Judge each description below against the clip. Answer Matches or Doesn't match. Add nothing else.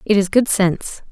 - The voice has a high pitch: Matches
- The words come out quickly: Matches